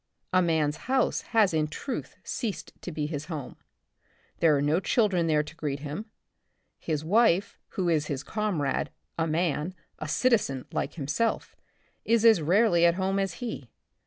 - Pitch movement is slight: No, average, 5.1 semitones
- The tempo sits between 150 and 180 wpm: Yes, average, 160 wpm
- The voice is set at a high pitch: No, medium, 170 Hz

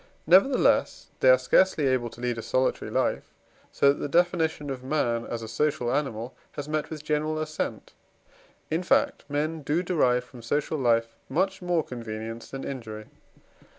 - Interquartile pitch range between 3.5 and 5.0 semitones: Yes, average, 4.7 semitones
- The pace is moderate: Yes, average, 165 wpm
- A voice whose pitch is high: No, medium, 140 Hz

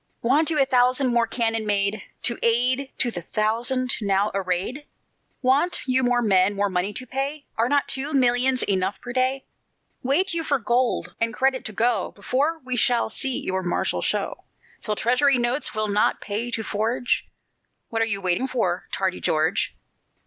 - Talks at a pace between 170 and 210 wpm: Yes, average, 175 wpm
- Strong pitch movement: No, average, 4.0 semitones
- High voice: Yes, high, 240 Hz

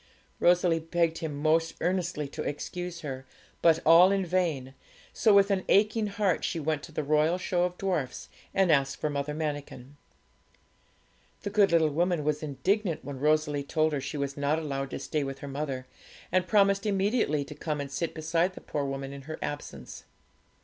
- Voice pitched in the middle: Yes, medium, 160 Hz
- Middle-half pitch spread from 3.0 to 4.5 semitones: Yes, average, 3.9 semitones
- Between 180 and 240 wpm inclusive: Yes, average, 185 wpm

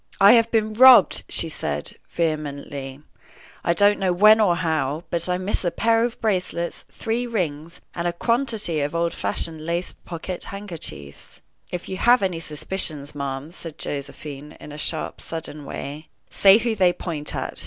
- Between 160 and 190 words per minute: Yes, average, 165 wpm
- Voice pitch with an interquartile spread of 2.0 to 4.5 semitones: No, average, 5.2 semitones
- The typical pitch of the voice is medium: Yes, medium, 170 Hz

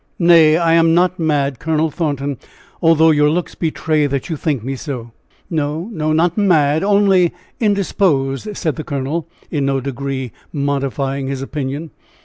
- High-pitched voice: No, medium, 155 Hz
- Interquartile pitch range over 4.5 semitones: No, average, 3.3 semitones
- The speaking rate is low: No, average, 150 wpm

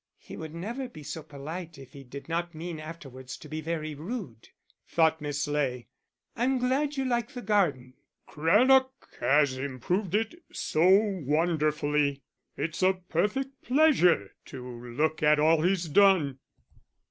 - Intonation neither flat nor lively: No, wide, 5.7 semitones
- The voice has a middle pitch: Yes, medium, 160 Hz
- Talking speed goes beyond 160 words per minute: No, average, 145 wpm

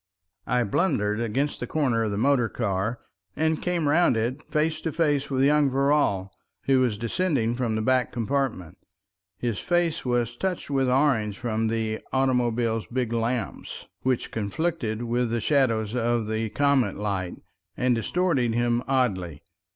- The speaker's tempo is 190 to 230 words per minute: No, average, 150 wpm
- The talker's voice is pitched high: No, low, 120 Hz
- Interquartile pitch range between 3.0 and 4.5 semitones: Yes, average, 3.9 semitones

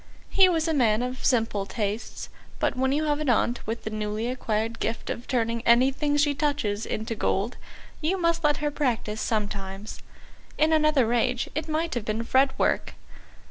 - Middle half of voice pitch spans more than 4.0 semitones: Yes, average, 5.2 semitones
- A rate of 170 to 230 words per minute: Yes, average, 175 wpm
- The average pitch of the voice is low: No, high, 245 Hz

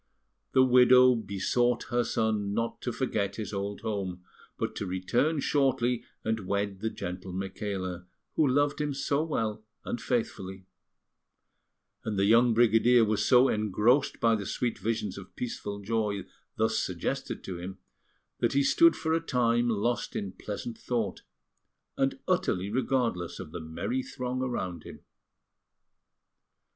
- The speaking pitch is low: Yes, low, 110 Hz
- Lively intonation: No, average, 4.0 semitones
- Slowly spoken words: No, average, 145 wpm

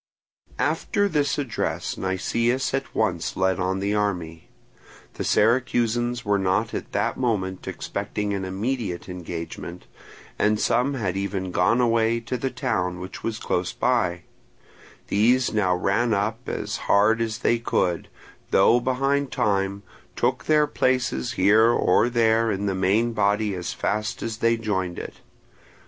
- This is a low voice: Yes, low, 105 Hz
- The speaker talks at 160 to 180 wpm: No, average, 145 wpm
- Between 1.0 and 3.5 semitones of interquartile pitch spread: No, average, 4.1 semitones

